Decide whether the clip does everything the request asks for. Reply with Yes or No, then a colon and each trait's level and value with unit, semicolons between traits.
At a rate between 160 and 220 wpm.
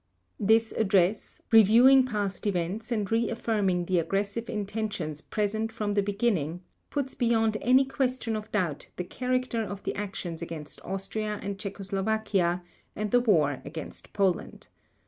No: average, 140 wpm